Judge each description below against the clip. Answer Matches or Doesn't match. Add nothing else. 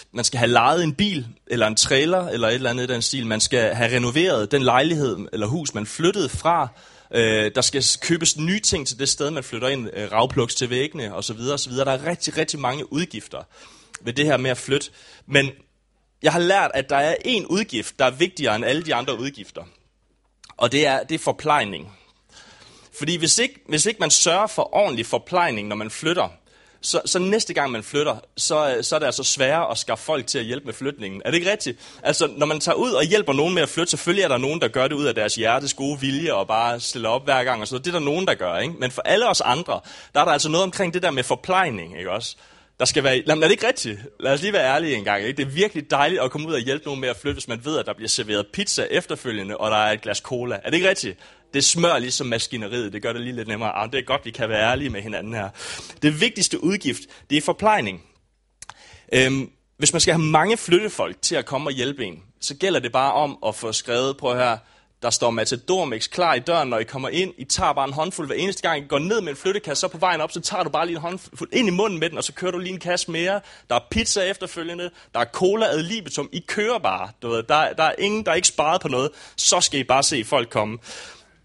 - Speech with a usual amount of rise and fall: Doesn't match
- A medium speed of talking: Doesn't match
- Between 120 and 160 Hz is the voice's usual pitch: Matches